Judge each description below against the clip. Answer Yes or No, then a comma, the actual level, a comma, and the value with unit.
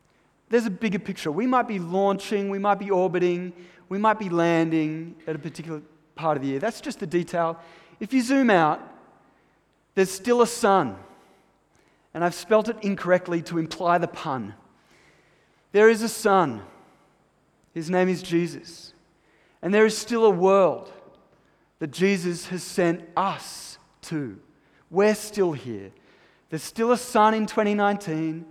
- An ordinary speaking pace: Yes, average, 155 wpm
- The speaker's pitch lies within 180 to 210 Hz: Yes, medium, 185 Hz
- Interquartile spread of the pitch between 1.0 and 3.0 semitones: No, average, 3.9 semitones